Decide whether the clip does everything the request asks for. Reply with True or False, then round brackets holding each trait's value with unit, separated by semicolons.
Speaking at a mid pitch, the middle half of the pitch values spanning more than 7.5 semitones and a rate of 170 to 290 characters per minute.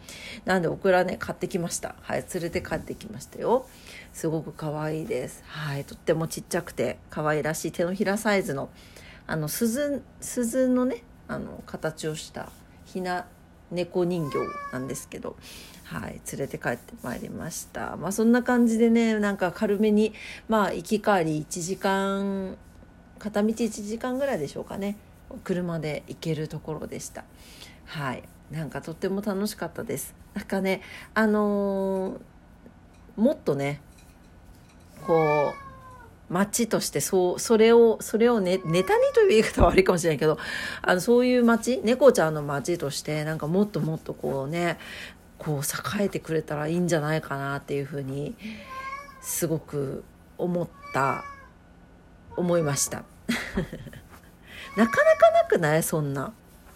False (180 Hz; 6.0 semitones; 285 characters per minute)